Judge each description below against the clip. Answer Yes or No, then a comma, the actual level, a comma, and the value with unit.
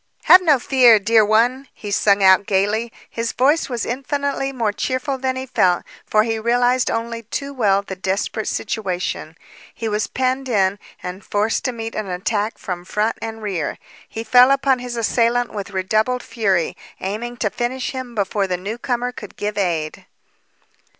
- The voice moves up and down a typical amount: Yes, average, 3.7 semitones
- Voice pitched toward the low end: No, high, 225 Hz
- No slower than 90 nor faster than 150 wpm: No, average, 170 wpm